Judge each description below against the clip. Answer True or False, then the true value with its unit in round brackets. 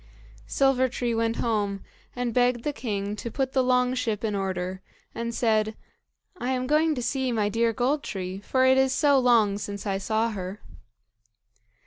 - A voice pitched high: True (235 Hz)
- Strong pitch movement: False (3.8 semitones)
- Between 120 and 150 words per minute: False (175 wpm)